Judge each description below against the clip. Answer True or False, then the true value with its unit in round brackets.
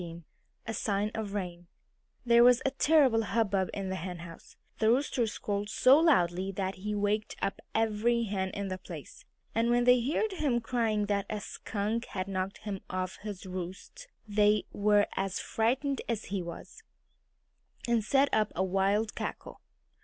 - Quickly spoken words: False (165 wpm)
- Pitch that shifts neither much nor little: True (3.6 semitones)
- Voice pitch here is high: True (210 Hz)